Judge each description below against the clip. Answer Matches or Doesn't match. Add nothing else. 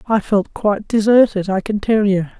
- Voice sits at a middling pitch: Doesn't match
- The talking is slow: Doesn't match